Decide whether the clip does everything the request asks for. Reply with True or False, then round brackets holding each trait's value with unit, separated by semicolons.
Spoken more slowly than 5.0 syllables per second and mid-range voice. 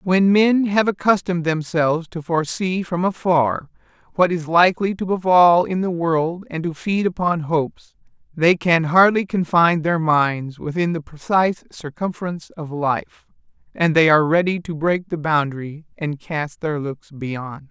True (4.6 syllables/s; 165 Hz)